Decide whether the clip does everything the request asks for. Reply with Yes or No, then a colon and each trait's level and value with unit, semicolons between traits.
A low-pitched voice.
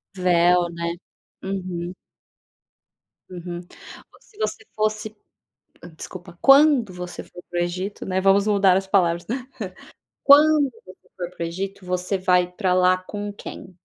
No: medium, 185 Hz